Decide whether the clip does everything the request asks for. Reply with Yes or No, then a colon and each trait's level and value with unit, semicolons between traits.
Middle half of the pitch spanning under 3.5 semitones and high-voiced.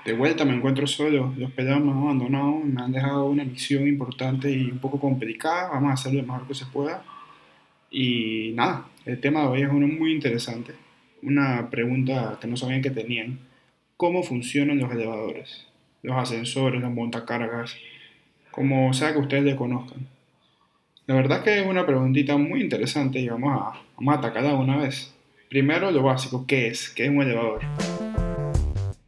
No: narrow, 2.4 semitones; low, 135 Hz